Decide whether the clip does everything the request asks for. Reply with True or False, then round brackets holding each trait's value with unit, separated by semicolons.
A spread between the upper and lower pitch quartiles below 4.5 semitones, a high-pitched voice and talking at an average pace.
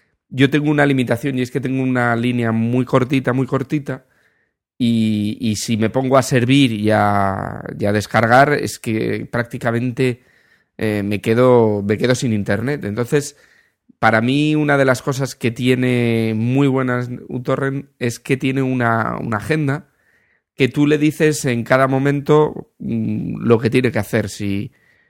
False (3.1 semitones; 125 Hz; 165 wpm)